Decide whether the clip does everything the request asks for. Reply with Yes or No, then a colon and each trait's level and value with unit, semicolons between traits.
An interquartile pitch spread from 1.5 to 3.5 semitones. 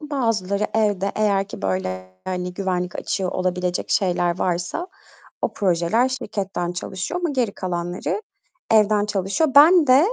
No: average, 3.9 semitones